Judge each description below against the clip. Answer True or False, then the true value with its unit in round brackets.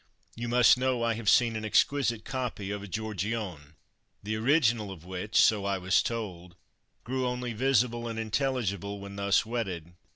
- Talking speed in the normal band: True (165 wpm)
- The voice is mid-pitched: False (110 Hz)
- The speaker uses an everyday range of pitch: True (3.3 semitones)